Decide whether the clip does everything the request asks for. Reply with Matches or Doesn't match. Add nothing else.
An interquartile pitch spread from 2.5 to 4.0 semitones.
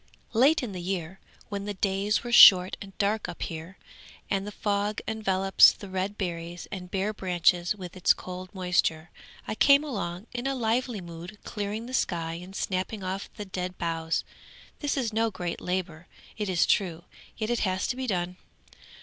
Matches